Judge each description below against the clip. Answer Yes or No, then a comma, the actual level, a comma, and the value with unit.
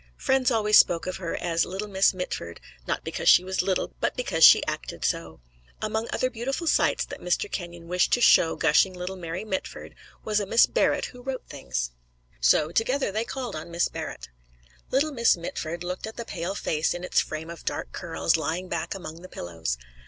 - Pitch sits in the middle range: Yes, medium, 180 Hz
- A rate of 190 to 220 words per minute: Yes, average, 195 wpm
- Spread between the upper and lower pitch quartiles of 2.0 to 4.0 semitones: No, average, 5.0 semitones